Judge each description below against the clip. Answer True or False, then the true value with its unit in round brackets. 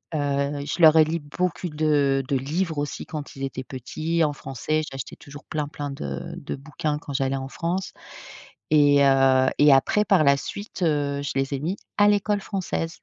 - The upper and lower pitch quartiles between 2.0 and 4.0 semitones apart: True (2.9 semitones)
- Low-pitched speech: False (145 Hz)